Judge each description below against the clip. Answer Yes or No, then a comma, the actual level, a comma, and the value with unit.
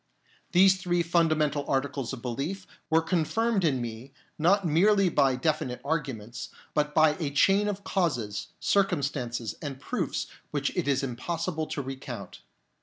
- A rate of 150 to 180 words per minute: No, average, 140 wpm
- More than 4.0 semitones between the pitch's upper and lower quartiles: Yes, average, 4.9 semitones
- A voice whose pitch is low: No, medium, 150 Hz